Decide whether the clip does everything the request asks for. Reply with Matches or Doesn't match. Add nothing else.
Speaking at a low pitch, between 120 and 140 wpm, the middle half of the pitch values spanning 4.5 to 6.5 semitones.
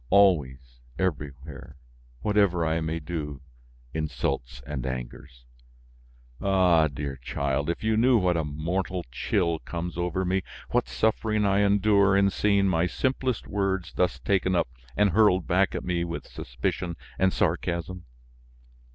Matches